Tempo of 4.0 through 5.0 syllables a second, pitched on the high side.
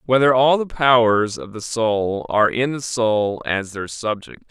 No: 4.2 syllables/s; low, 115 Hz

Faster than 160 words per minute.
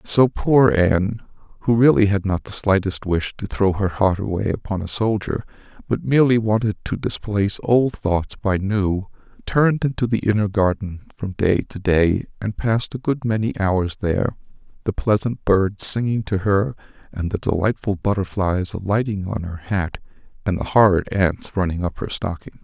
Yes: average, 170 wpm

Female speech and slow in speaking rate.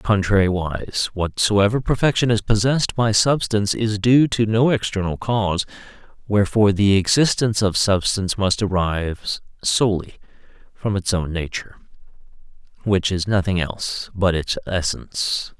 No: male; slow, 125 wpm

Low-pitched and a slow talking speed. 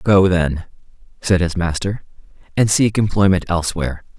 Yes: very low, 90 Hz; slow, 130 wpm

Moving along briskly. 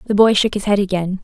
Yes: fast, 290 wpm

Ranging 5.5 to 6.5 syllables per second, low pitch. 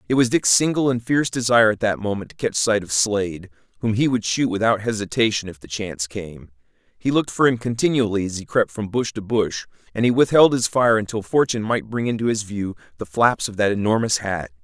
Yes: 5.9 syllables/s; low, 110 Hz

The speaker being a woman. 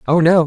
No: male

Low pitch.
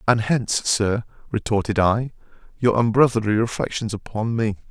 Yes: low, 110 Hz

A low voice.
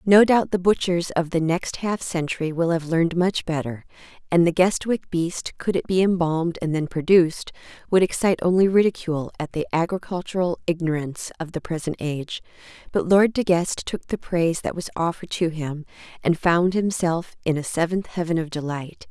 No: medium, 170 Hz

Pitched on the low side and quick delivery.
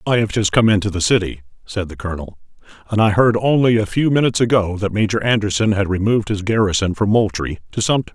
Yes: low, 105 Hz; fast, 215 wpm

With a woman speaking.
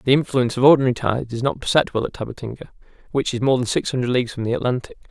No: male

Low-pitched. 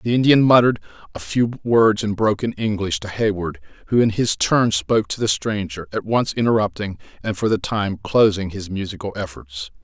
Yes: low, 105 Hz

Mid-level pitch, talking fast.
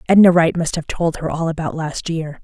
Yes: medium, 165 Hz; fast, 245 wpm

